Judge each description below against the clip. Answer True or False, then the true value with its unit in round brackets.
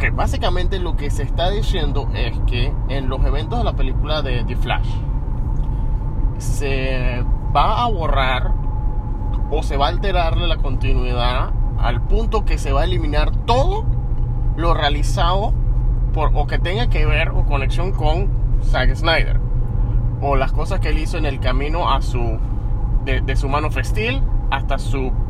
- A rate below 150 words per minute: False (160 wpm)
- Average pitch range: False (2.3 semitones)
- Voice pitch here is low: True (120 Hz)